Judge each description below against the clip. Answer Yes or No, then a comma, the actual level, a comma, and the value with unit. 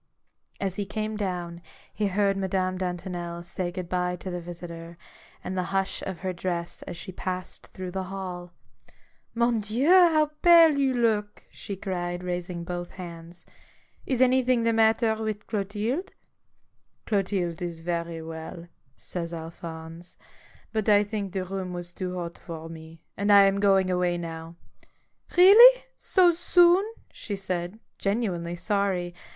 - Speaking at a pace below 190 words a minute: Yes, average, 160 wpm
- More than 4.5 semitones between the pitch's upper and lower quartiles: No, average, 3.5 semitones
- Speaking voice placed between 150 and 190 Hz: Yes, medium, 185 Hz